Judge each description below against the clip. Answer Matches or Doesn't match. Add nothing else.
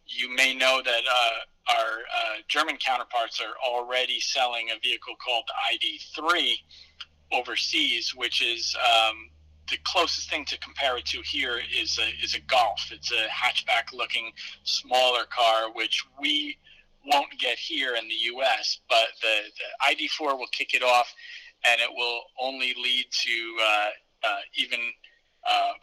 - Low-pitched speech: Matches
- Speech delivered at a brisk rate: Doesn't match